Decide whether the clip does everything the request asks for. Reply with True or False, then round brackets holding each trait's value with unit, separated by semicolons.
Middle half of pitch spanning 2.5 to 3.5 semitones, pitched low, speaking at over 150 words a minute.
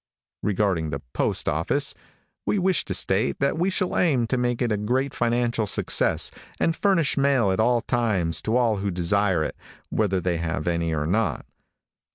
False (5.6 semitones; 110 Hz; 175 wpm)